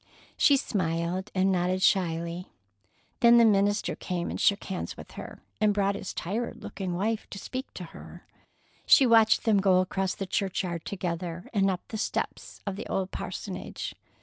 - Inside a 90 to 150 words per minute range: No, average, 170 wpm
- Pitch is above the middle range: Yes, high, 195 Hz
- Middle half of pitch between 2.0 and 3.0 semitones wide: Yes, narrow, 2.6 semitones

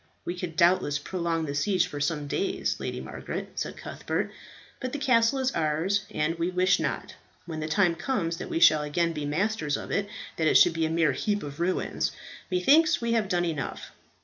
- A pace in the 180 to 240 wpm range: Yes, average, 200 wpm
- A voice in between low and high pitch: Yes, medium, 175 Hz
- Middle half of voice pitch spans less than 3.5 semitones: No, average, 4.4 semitones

